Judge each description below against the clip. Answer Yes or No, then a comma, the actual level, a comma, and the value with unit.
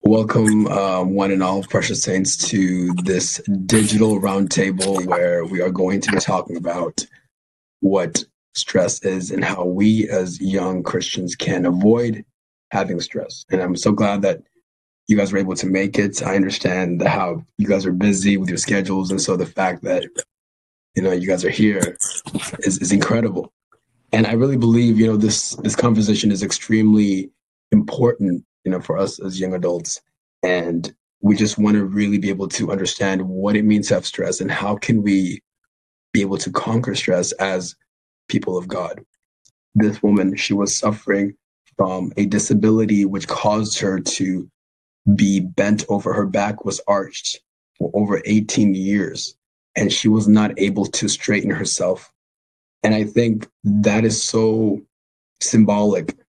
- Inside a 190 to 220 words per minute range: No, average, 165 wpm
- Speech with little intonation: Yes, narrow, 2.3 semitones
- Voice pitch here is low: Yes, low, 100 Hz